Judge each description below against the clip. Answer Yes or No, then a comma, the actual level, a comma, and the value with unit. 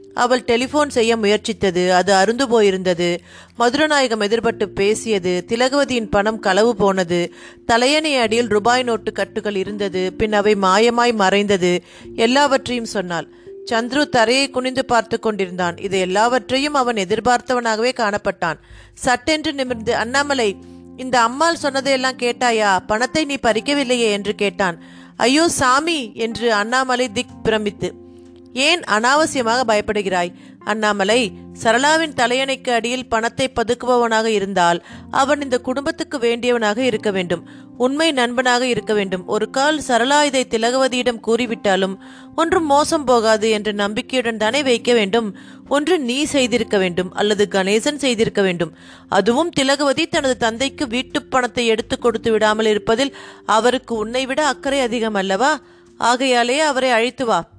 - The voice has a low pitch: No, high, 235 Hz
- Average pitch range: Yes, average, 4.0 semitones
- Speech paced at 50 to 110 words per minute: No, average, 120 wpm